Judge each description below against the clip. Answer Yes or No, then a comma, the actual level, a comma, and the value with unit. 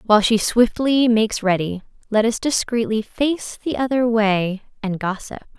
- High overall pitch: Yes, high, 225 Hz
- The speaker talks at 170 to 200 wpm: No, average, 150 wpm